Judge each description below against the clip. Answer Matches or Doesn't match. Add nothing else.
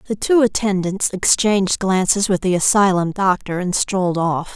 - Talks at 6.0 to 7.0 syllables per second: Doesn't match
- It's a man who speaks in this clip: Doesn't match